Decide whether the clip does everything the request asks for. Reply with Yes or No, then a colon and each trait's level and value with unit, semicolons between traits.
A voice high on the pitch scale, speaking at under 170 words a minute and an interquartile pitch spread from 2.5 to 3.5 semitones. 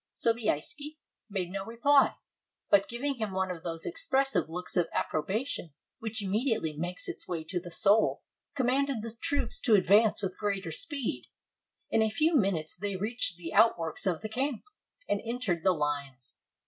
No: high, 205 Hz; average, 160 wpm; wide, 5.4 semitones